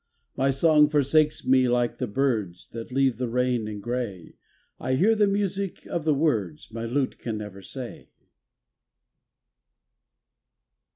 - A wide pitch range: No, average, 4.7 semitones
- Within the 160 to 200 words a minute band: No, slow, 135 wpm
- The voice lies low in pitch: Yes, low, 130 Hz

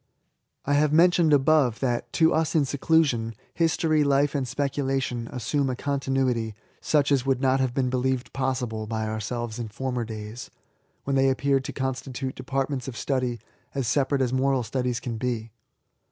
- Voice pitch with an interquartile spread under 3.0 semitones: Yes, narrow, 2.5 semitones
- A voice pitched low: Yes, low, 130 Hz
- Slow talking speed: No, average, 165 wpm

